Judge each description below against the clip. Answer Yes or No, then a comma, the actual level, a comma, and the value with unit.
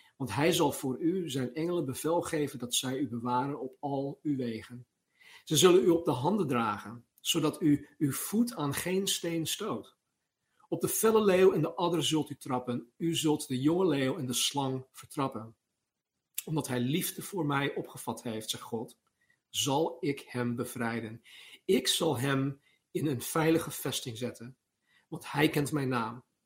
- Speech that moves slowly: No, average, 175 wpm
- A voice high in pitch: No, medium, 140 Hz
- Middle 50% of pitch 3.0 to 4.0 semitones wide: No, average, 4.7 semitones